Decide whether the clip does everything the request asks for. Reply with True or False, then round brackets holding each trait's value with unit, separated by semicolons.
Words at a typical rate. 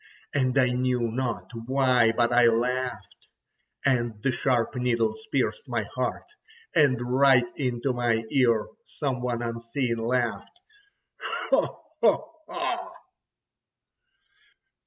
False (105 wpm)